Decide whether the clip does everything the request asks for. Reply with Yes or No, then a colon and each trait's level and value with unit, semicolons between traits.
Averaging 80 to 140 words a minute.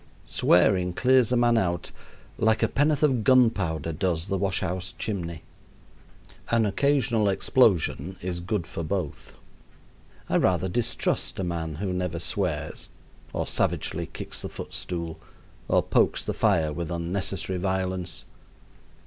Yes: slow, 135 wpm